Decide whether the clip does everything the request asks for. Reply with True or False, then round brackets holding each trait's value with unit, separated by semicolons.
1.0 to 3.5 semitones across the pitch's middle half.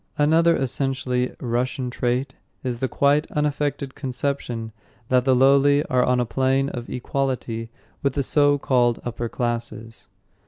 True (2.4 semitones)